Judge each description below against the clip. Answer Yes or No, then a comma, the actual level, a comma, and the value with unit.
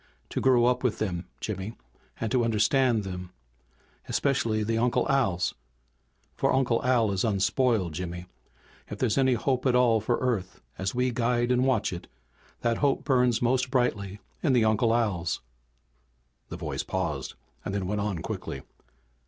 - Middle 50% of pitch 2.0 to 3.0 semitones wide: No, average, 3.8 semitones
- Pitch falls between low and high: No, low, 115 Hz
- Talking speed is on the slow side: No, average, 155 wpm